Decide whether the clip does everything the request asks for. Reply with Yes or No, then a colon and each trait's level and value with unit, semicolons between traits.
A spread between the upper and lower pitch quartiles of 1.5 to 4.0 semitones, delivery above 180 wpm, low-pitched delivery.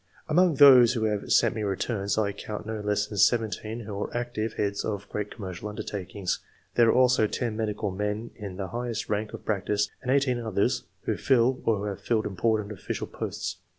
Yes: narrow, 2.6 semitones; average, 190 wpm; low, 110 Hz